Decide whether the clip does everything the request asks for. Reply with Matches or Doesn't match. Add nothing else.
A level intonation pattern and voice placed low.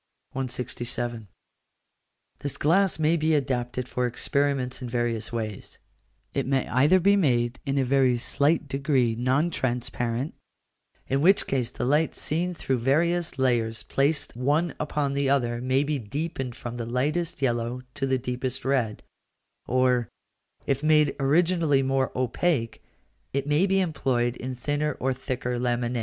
Doesn't match